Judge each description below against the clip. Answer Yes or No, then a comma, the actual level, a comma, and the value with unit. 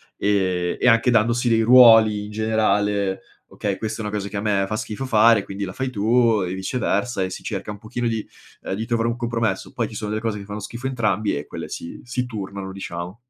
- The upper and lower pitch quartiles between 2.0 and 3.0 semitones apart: Yes, narrow, 2.6 semitones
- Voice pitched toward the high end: No, low, 105 Hz